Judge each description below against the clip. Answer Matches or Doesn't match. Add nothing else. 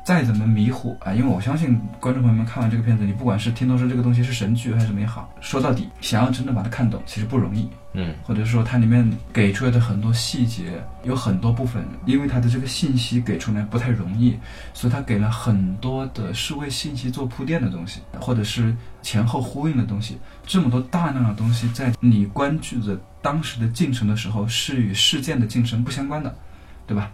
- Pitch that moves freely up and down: Doesn't match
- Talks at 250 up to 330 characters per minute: Doesn't match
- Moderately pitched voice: Doesn't match